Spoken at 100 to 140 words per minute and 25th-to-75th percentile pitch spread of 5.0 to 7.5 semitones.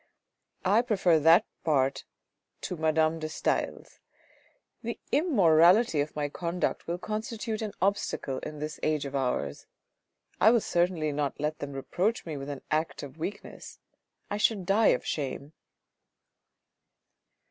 Yes: slow, 135 wpm; wide, 5.6 semitones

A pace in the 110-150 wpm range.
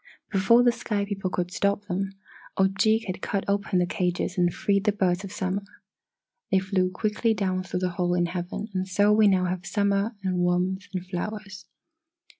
No: average, 185 wpm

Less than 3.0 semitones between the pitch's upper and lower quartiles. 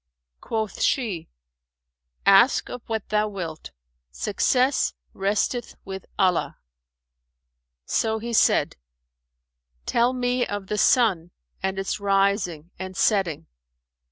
No: average, 3.5 semitones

